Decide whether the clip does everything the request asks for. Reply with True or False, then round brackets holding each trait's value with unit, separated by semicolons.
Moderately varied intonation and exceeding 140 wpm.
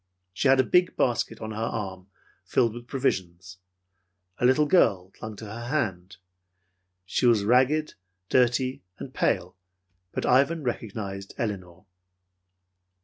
False (4.9 semitones; 135 wpm)